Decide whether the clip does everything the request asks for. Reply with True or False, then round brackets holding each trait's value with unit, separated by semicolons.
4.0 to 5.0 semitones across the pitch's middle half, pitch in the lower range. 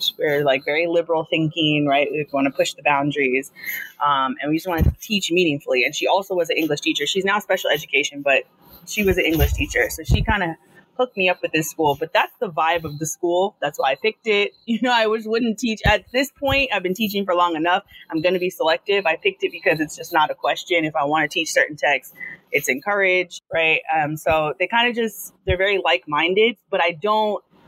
False (4.5 semitones; 180 Hz)